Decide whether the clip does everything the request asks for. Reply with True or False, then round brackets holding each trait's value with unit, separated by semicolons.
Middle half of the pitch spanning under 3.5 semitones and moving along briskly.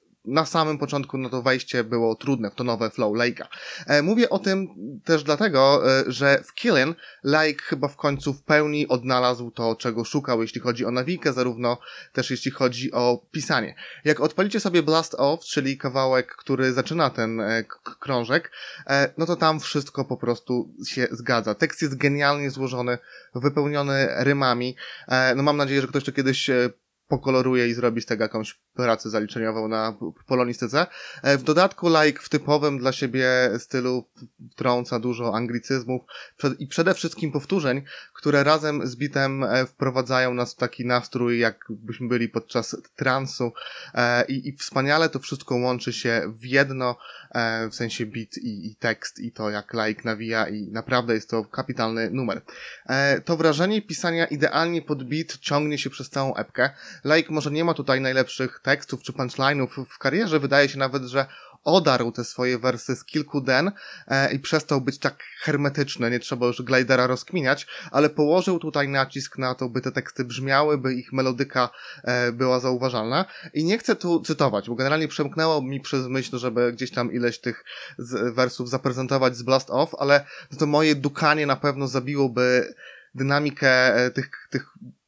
True (3.0 semitones; 165 wpm)